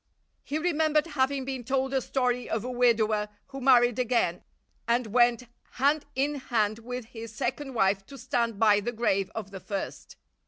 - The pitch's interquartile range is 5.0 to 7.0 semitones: No, average, 3.2 semitones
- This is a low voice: No, high, 245 Hz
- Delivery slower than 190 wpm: Yes, average, 170 wpm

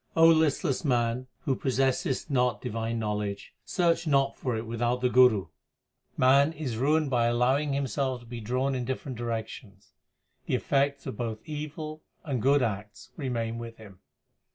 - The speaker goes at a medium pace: Yes, average, 155 wpm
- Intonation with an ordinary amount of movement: Yes, average, 3.2 semitones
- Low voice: Yes, low, 125 Hz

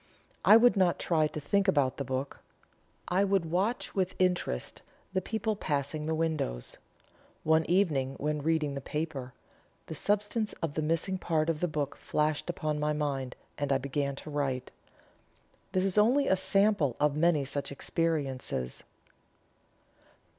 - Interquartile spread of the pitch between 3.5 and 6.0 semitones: Yes, average, 4.7 semitones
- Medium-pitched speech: Yes, medium, 155 Hz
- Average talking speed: Yes, average, 155 wpm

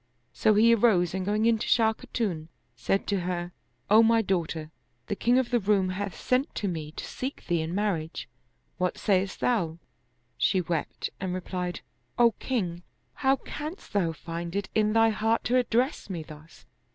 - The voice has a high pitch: Yes, high, 200 Hz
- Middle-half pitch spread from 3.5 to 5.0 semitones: Yes, average, 4.6 semitones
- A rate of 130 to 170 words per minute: No, average, 180 wpm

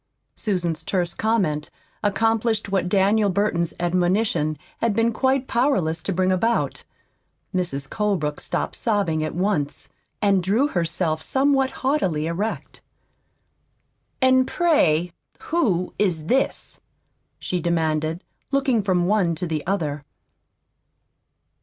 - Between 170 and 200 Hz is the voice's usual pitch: Yes, high, 190 Hz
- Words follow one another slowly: Yes, slow, 110 wpm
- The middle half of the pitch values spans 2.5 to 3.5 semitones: No, average, 5.1 semitones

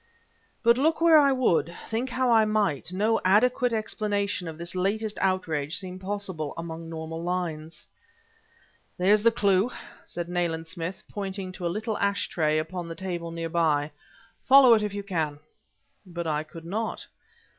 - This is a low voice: No, medium, 185 Hz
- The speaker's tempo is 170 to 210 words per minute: No, average, 160 wpm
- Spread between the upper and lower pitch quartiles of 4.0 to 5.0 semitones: Yes, average, 4.4 semitones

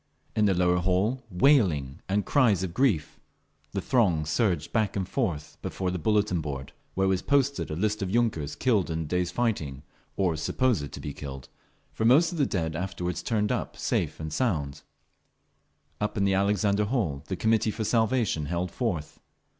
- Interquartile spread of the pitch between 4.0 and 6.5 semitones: Yes, wide, 5.5 semitones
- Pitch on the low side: Yes, very low, 95 Hz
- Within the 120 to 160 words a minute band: No, average, 175 wpm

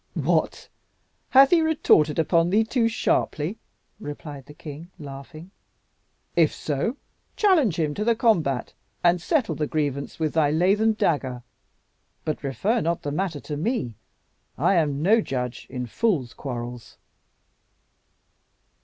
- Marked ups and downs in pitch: Yes, wide, 7.0 semitones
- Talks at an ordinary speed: No, slow, 130 wpm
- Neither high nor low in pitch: Yes, medium, 160 Hz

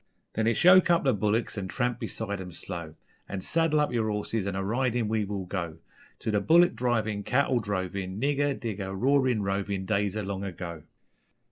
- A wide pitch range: No, average, 4.2 semitones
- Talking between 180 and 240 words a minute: Yes, average, 190 wpm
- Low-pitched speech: Yes, low, 105 Hz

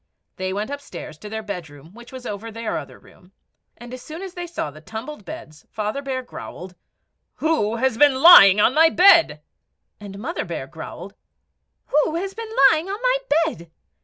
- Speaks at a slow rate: No, average, 180 wpm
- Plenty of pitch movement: Yes, wide, 8.0 semitones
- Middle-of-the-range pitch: No, high, 245 Hz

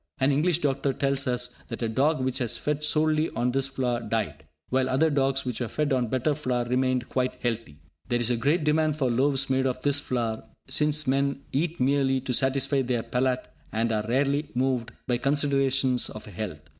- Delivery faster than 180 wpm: Yes, average, 195 wpm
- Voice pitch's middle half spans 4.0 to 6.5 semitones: No, narrow, 2.5 semitones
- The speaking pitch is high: No, low, 130 Hz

